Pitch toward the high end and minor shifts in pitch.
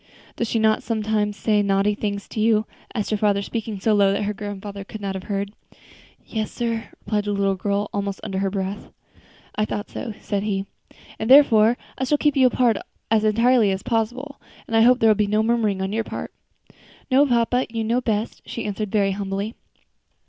Yes: high, 215 Hz; narrow, 2.2 semitones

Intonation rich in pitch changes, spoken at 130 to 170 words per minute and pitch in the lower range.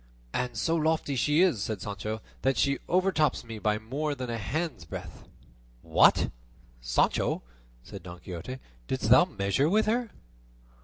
Yes: wide, 7.6 semitones; average, 150 wpm; low, 125 Hz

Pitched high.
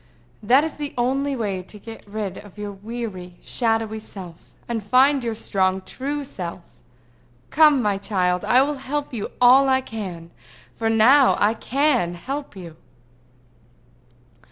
Yes: high, 225 Hz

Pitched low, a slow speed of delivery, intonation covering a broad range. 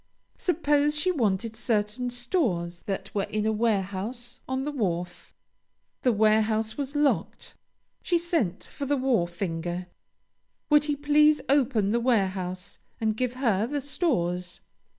No: high, 230 Hz; slow, 130 wpm; wide, 6.6 semitones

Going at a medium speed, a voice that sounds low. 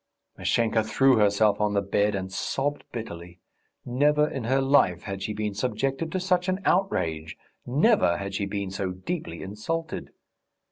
Yes: average, 155 wpm; low, 110 Hz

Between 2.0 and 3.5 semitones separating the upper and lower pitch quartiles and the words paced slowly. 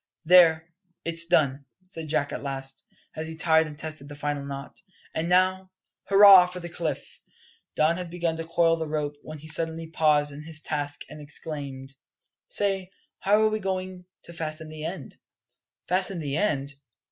No: average, 3.2 semitones; average, 170 wpm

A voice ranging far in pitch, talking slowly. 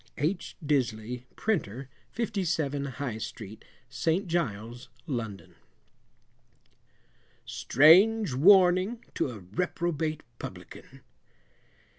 Yes: wide, 7.1 semitones; slow, 75 wpm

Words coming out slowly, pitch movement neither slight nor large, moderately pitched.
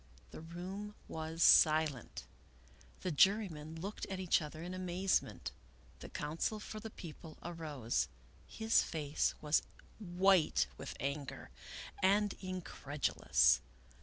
Yes: slow, 115 wpm; average, 3.9 semitones; medium, 170 Hz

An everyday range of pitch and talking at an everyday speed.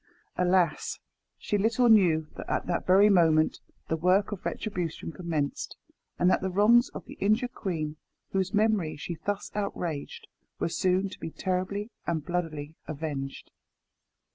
Yes: average, 4.1 semitones; average, 145 wpm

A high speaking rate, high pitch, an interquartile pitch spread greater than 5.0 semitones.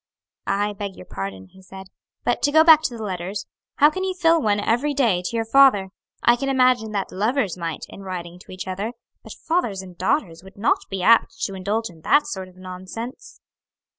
Yes: fast, 210 wpm; high, 205 Hz; wide, 5.5 semitones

